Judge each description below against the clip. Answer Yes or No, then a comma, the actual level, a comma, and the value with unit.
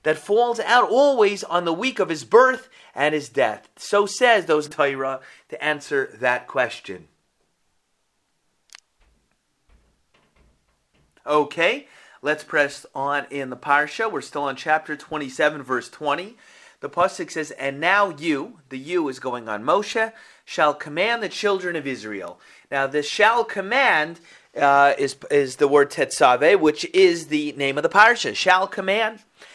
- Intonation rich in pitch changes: Yes, wide, 6.6 semitones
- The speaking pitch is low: No, medium, 155 Hz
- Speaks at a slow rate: No, average, 145 wpm